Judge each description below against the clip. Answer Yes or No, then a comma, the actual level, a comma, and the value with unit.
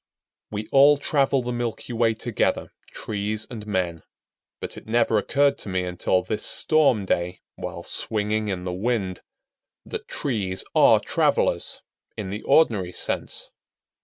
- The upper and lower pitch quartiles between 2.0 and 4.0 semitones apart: No, average, 4.5 semitones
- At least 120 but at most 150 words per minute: Yes, average, 140 wpm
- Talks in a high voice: No, low, 110 Hz